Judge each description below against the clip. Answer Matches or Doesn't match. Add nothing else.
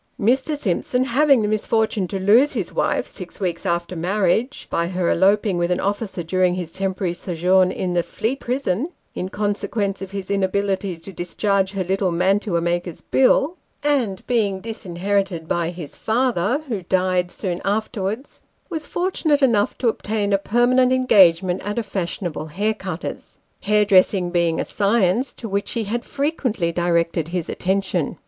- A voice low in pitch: Doesn't match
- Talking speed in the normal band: Matches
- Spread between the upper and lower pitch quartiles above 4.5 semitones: Doesn't match